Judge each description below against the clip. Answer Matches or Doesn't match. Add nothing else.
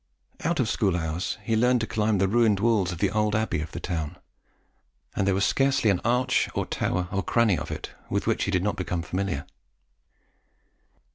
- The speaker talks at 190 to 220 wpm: Matches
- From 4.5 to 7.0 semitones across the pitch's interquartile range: Doesn't match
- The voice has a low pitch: Matches